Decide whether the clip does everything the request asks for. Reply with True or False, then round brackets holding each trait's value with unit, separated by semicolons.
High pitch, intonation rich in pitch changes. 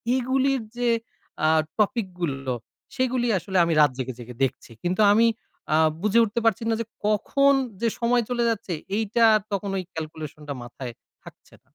True (210 Hz; 7.4 semitones)